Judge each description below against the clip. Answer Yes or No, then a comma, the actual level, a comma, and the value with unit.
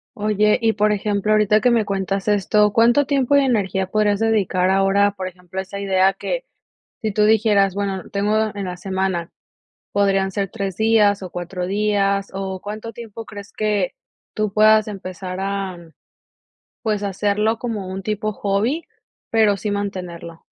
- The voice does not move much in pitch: Yes, narrow, 1.8 semitones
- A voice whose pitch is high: Yes, high, 205 Hz